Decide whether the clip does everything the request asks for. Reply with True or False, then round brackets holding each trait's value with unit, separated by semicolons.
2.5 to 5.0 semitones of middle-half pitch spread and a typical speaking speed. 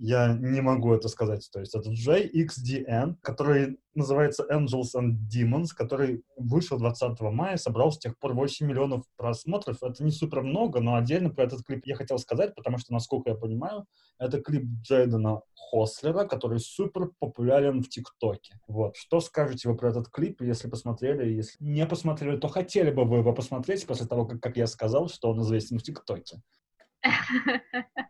False (4.2 semitones; 170 wpm)